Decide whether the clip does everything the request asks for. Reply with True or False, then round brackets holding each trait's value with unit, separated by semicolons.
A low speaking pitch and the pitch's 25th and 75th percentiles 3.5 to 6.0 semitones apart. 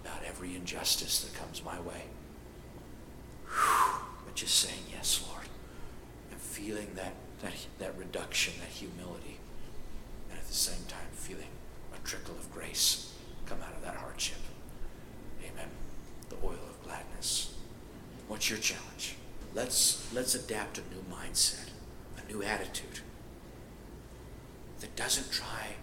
True (95 Hz; 5.4 semitones)